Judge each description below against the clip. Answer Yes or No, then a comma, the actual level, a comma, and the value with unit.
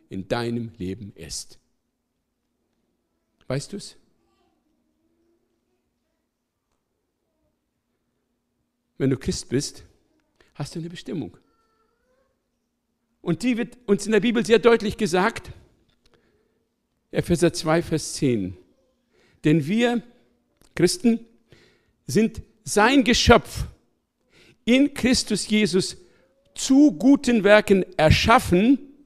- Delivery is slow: Yes, slow, 85 wpm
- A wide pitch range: Yes, wide, 7.2 semitones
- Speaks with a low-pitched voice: No, high, 210 Hz